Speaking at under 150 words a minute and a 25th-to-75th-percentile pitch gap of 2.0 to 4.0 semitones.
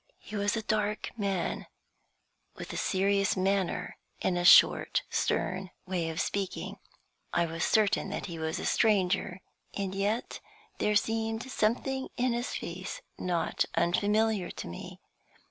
Yes: average, 140 wpm; average, 3.0 semitones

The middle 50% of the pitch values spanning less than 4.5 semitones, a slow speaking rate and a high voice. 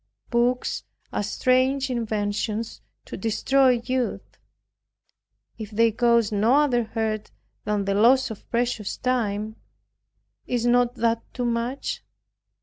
Yes: narrow, 2.6 semitones; slow, 115 wpm; high, 235 Hz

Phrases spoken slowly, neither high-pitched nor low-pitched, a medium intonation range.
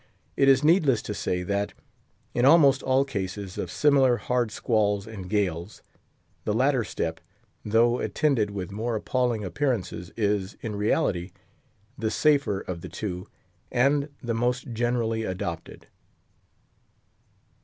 No: slow, 130 wpm; low, 110 Hz; average, 4.6 semitones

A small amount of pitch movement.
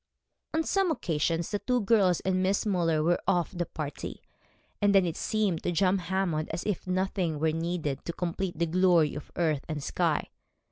No: average, 3.1 semitones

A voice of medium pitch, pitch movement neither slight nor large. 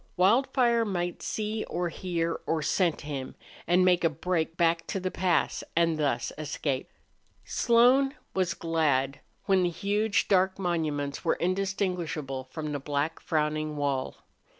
Yes: medium, 170 Hz; average, 3.8 semitones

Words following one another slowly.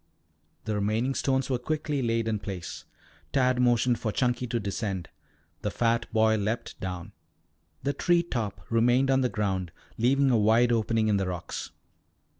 No: average, 160 wpm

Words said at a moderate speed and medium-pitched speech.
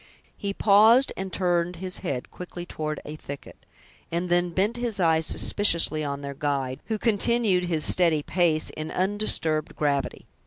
Yes: average, 155 wpm; medium, 175 Hz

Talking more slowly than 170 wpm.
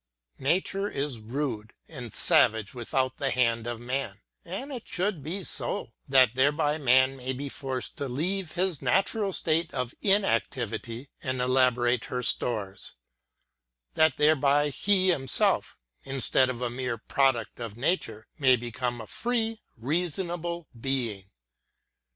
Yes: slow, 135 wpm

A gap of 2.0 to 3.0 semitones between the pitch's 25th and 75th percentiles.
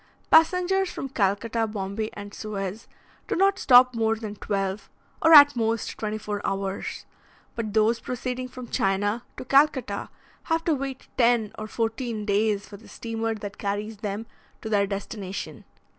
No: average, 3.6 semitones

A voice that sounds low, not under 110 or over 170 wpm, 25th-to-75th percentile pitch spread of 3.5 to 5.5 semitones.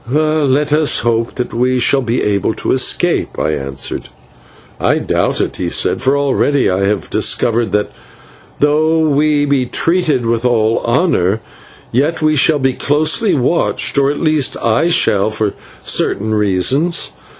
Yes: low, 130 Hz; average, 150 wpm; average, 5.2 semitones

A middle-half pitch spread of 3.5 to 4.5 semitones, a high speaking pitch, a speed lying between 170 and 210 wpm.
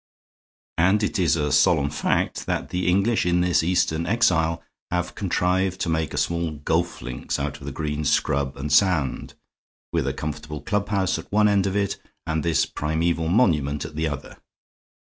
No: average, 3.8 semitones; very low, 80 Hz; average, 175 wpm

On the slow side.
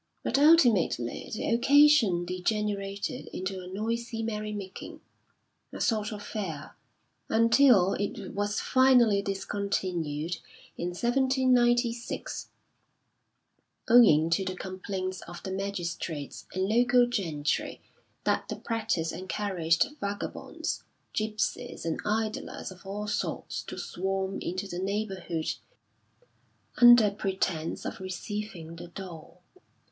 Yes: slow, 105 wpm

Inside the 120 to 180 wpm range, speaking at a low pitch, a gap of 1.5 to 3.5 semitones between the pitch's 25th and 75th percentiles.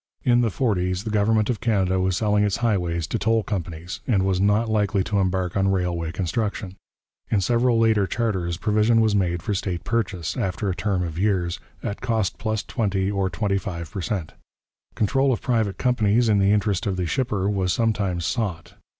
No: average, 190 wpm; low, 100 Hz; average, 3.2 semitones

